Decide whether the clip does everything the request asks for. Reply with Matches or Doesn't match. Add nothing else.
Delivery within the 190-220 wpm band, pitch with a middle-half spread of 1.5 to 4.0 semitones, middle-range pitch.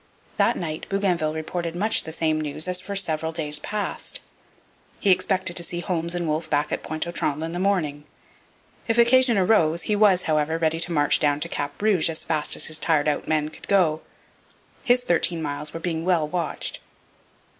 Matches